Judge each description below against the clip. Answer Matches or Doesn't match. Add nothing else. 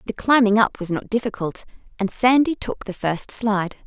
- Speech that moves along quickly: Doesn't match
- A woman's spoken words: Matches